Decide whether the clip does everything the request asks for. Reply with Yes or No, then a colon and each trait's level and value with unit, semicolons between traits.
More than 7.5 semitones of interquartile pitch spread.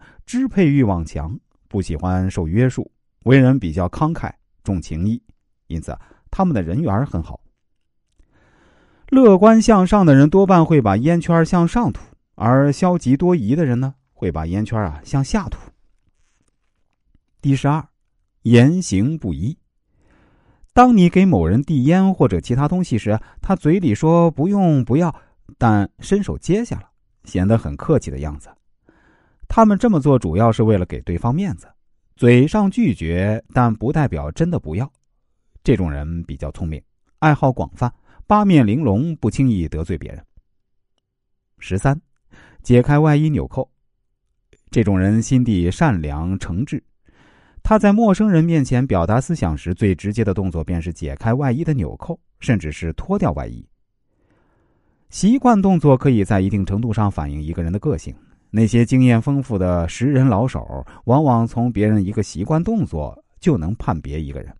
Yes: wide, 8.9 semitones